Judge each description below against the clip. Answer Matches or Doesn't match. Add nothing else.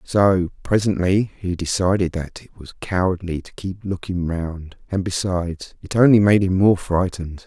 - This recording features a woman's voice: Doesn't match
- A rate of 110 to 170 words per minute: Matches